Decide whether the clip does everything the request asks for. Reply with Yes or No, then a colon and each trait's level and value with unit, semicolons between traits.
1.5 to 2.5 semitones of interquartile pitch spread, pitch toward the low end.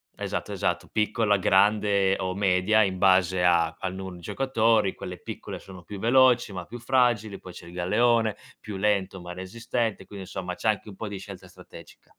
No: average, 2.9 semitones; low, 100 Hz